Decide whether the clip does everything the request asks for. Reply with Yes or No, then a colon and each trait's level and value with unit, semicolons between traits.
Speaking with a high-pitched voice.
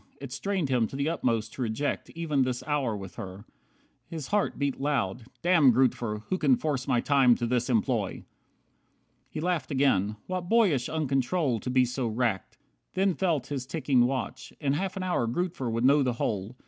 No: low, 130 Hz